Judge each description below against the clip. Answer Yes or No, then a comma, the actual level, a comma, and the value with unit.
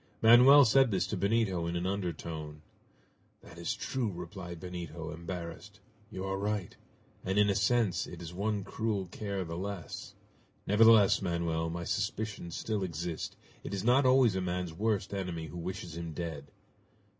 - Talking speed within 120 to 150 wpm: No, average, 160 wpm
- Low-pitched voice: Yes, very low, 95 Hz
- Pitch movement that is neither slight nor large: Yes, average, 3.5 semitones